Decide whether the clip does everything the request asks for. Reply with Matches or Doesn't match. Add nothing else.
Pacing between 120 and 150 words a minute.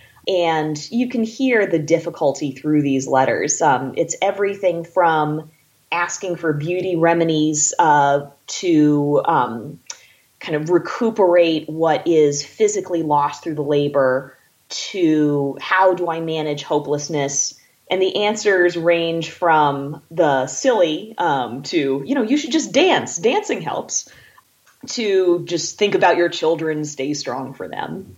Matches